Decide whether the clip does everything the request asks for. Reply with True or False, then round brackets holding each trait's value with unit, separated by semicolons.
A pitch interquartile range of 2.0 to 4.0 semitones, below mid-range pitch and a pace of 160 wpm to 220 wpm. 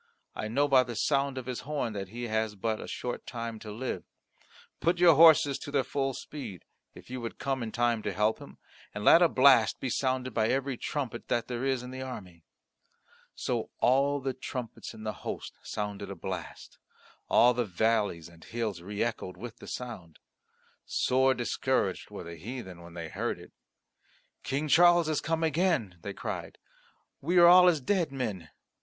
False (4.4 semitones; 125 Hz; 185 wpm)